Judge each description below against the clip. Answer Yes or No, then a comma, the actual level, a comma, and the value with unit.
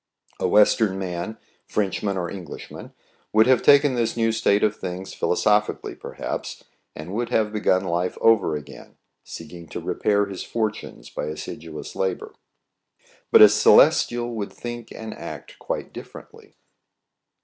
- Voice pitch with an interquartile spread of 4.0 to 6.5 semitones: No, average, 3.5 semitones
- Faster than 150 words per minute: No, average, 140 wpm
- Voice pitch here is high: No, low, 105 Hz